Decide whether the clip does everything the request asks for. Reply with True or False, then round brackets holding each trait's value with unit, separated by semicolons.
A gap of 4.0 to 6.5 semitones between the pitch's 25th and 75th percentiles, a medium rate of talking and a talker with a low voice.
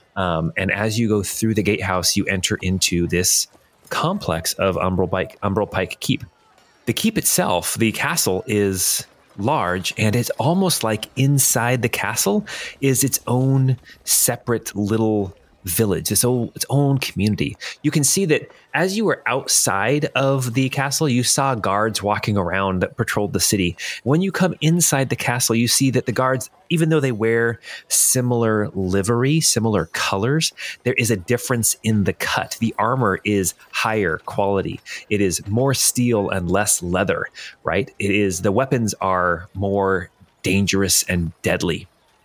True (5.1 semitones; 160 wpm; 110 Hz)